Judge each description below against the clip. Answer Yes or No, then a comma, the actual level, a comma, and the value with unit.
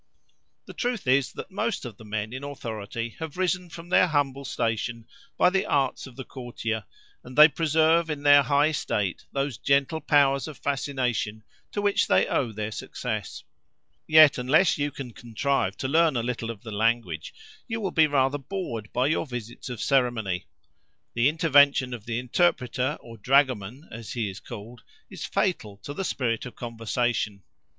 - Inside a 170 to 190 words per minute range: Yes, average, 175 wpm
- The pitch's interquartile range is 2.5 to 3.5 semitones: No, average, 4.3 semitones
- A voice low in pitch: Yes, low, 130 Hz